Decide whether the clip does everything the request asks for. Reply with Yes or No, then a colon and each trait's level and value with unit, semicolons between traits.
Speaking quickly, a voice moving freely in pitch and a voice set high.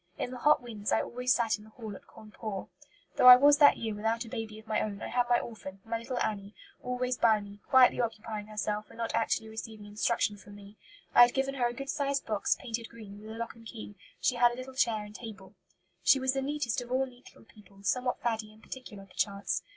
No: fast, 240 wpm; average, 2.9 semitones; high, 225 Hz